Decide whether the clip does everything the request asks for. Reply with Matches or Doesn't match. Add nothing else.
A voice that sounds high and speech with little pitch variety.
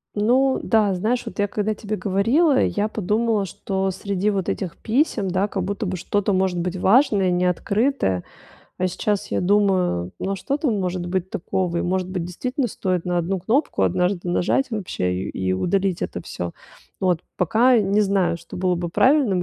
Doesn't match